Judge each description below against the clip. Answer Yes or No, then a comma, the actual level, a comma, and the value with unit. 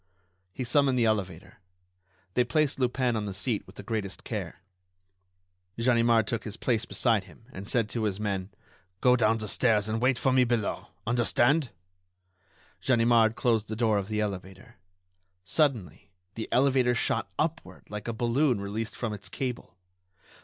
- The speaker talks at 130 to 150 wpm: No, average, 160 wpm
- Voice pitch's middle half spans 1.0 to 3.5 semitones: Yes, average, 2.9 semitones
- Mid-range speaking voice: No, low, 115 Hz